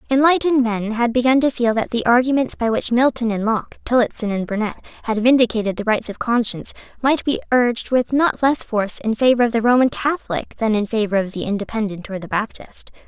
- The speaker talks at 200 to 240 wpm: Yes, fast, 205 wpm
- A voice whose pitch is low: No, high, 230 Hz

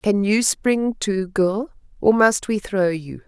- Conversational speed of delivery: Yes, average, 185 wpm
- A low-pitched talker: No, high, 205 Hz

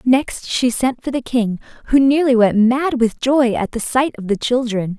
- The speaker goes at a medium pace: No, fast, 215 wpm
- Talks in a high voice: Yes, high, 245 Hz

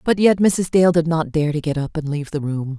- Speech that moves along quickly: Yes, fast, 300 wpm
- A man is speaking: No, female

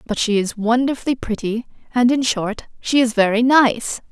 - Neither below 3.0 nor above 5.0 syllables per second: Yes, 4.9 syllables/s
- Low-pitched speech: No, high, 235 Hz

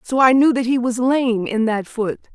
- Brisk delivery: Yes, fast, 255 wpm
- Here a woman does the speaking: Yes, female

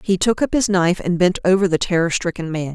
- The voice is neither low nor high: Yes, medium, 180 Hz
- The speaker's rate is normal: No, fast, 265 wpm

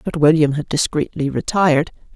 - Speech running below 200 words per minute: Yes, average, 140 wpm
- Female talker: Yes, female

